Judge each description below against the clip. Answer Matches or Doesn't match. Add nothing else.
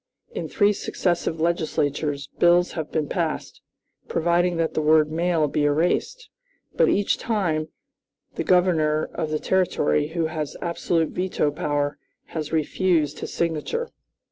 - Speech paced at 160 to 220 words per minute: Doesn't match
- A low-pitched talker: Doesn't match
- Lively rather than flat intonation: Doesn't match